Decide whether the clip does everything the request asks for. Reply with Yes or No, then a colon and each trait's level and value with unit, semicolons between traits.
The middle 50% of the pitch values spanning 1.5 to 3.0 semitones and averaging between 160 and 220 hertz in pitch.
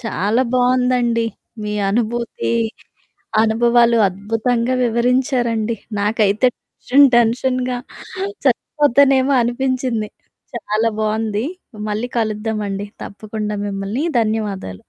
No: average, 2.7 semitones; high, 230 Hz